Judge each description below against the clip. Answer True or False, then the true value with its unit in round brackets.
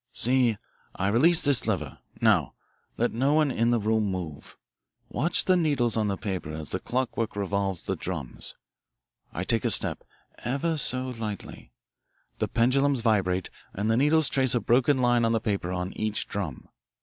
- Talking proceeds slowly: False (170 wpm)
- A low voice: True (115 Hz)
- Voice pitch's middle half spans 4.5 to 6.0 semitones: True (5.0 semitones)